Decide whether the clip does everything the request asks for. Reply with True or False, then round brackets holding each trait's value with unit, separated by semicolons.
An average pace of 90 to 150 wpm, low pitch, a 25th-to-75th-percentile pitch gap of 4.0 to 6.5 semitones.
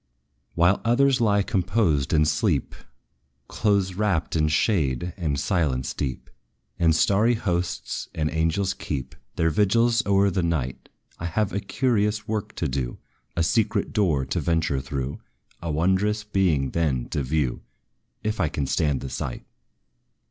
True (145 wpm; 85 Hz; 5.6 semitones)